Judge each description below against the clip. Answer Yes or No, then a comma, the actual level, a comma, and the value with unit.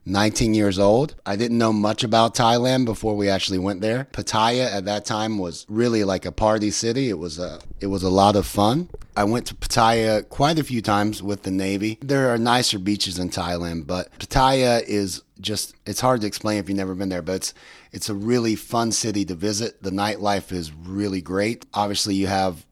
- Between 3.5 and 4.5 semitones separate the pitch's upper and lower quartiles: No, average, 2.8 semitones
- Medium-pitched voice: No, low, 105 Hz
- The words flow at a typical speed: No, fast, 210 wpm